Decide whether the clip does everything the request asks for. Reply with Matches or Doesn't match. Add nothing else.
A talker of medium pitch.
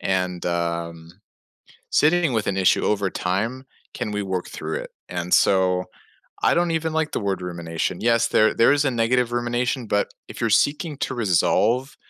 Doesn't match